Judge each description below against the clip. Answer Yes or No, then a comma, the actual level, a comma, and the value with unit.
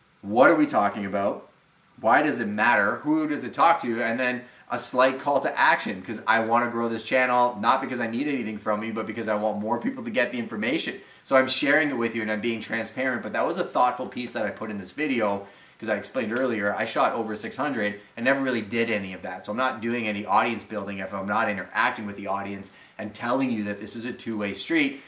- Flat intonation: No, average, 3.0 semitones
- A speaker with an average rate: No, fast, 255 wpm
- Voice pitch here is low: Yes, low, 115 Hz